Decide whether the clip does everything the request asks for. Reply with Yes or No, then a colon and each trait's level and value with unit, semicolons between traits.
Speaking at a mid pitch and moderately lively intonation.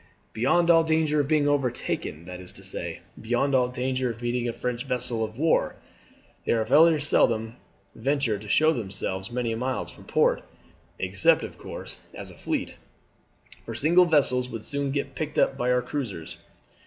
No: low, 125 Hz; average, 4.3 semitones